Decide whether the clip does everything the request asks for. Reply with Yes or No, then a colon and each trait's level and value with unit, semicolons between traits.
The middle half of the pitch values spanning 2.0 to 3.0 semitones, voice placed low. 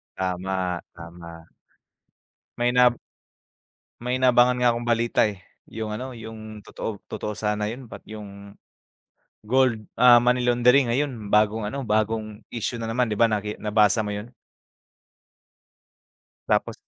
Yes: narrow, 2.6 semitones; low, 110 Hz